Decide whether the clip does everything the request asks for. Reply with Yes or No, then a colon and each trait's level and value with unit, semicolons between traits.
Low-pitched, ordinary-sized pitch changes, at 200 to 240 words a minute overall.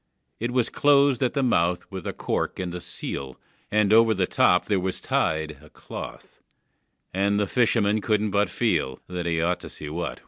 Yes: low, 100 Hz; average, 4.1 semitones; fast, 205 wpm